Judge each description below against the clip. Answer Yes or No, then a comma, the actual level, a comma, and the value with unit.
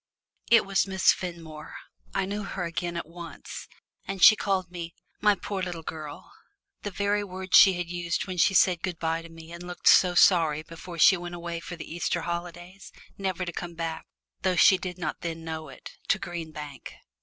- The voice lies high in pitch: No, medium, 175 Hz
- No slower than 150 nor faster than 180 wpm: No, average, 200 wpm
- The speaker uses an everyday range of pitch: No, narrow, 2.1 semitones